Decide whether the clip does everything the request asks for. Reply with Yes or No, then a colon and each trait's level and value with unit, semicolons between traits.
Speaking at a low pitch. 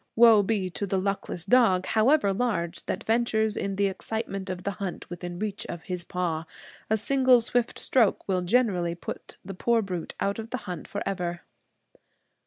No: high, 195 Hz